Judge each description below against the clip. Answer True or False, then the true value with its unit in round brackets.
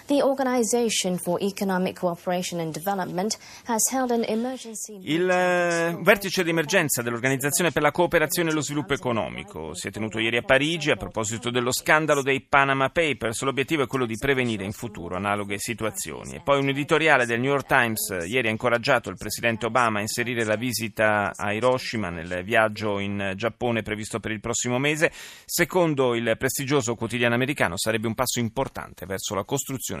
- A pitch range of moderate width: False (7.2 semitones)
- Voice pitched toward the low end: True (130 Hz)